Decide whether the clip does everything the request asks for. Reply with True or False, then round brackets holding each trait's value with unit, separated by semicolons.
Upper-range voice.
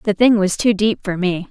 True (200 Hz)